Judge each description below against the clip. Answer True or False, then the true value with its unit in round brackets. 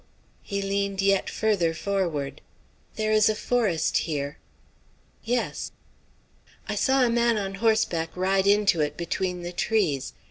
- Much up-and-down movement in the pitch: False (4.1 semitones)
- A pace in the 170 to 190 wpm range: False (135 wpm)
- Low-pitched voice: False (195 Hz)